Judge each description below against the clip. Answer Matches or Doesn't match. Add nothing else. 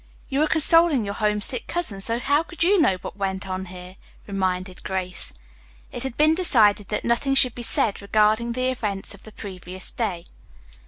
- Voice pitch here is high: Matches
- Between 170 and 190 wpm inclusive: Matches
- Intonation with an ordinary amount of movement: Doesn't match